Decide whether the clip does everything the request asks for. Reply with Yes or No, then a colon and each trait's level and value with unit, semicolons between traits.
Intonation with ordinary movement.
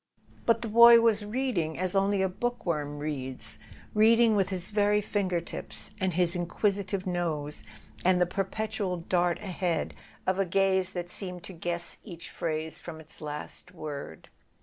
Yes: average, 3.3 semitones